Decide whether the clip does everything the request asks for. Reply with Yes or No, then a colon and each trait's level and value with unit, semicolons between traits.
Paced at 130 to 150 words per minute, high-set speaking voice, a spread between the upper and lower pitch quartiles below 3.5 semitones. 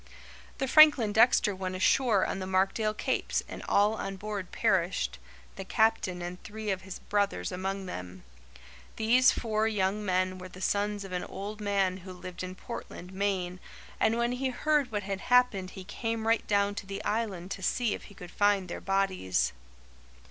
No: average, 180 wpm; high, 200 Hz; average, 2.8 semitones